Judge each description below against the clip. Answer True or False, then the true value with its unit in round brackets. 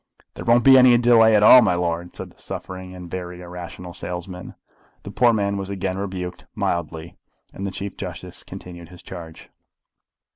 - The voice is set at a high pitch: False (95 Hz)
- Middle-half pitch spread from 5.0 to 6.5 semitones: False (2.4 semitones)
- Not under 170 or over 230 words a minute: True (175 wpm)